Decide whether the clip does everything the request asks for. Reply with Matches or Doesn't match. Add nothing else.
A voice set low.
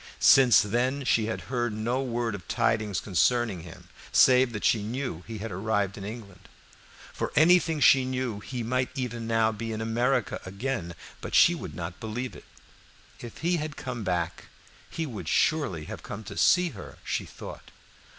Matches